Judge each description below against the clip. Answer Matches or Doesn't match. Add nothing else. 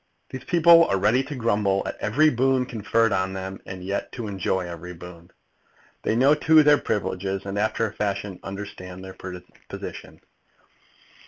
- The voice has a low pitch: Matches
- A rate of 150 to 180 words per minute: Matches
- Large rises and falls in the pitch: Doesn't match